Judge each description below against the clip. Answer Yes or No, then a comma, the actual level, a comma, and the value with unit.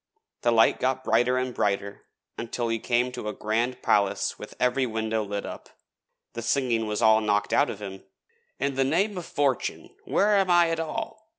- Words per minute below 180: No, average, 190 wpm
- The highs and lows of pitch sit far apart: No, average, 4.3 semitones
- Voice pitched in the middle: No, low, 120 Hz